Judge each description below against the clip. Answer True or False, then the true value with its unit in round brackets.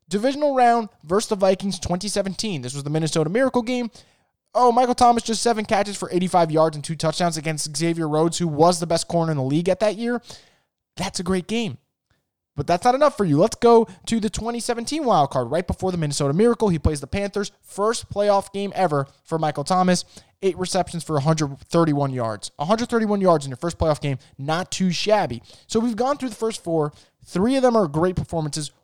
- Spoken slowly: False (205 wpm)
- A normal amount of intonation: False (5.7 semitones)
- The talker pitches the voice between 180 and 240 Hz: True (185 Hz)